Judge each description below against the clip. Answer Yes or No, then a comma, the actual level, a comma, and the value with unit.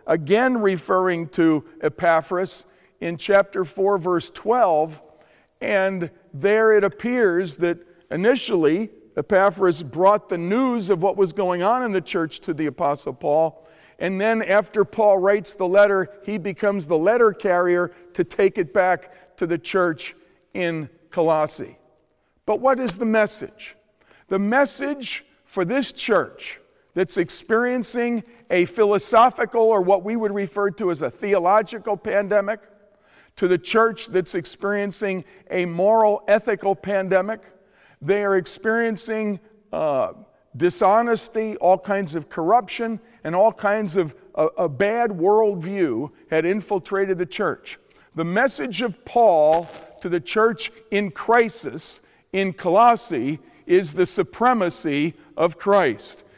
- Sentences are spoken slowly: Yes, slow, 130 wpm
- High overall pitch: Yes, high, 195 Hz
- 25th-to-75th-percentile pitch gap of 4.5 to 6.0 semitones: No, average, 3.7 semitones